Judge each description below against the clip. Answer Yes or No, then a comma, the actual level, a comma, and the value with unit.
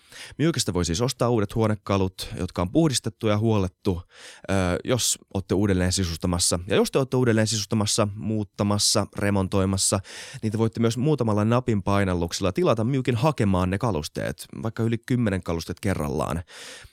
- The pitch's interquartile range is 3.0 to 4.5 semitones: Yes, average, 3.5 semitones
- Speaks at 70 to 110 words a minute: No, average, 140 wpm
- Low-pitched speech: Yes, low, 105 Hz